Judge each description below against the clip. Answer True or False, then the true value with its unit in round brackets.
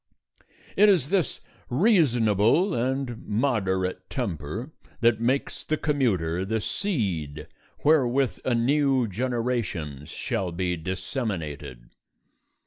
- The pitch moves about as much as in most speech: False (6.6 semitones)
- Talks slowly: True (95 wpm)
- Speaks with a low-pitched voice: True (115 Hz)